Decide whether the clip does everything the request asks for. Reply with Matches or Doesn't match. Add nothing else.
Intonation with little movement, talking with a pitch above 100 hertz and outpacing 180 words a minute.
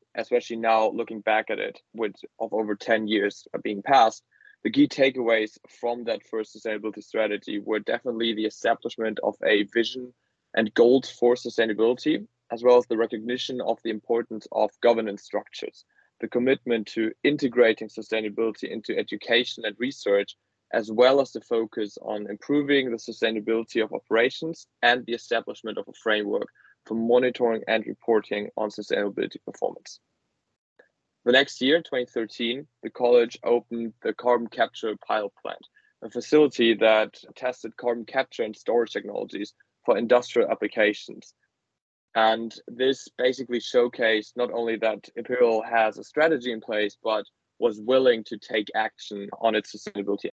Doesn't match